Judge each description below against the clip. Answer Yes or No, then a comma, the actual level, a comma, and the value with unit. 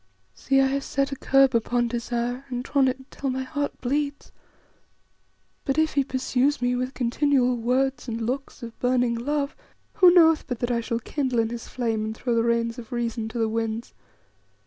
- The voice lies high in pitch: Yes, very high, 250 Hz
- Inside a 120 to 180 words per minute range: No, average, 190 wpm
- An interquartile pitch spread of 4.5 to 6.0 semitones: No, narrow, 2.6 semitones